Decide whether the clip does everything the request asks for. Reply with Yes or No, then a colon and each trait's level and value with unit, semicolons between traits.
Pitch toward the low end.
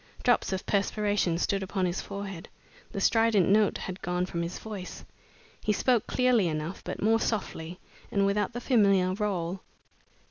No: high, 195 Hz